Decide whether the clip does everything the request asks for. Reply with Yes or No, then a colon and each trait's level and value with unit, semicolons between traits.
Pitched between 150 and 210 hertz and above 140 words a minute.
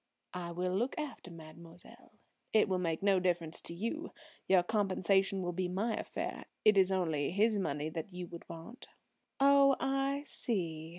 Yes: medium, 185 Hz; average, 165 wpm